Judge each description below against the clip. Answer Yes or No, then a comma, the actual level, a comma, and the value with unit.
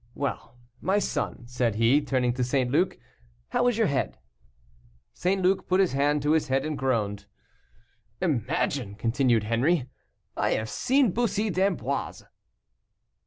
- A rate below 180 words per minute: Yes, average, 140 wpm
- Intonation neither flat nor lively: No, wide, 7.0 semitones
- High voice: No, medium, 140 Hz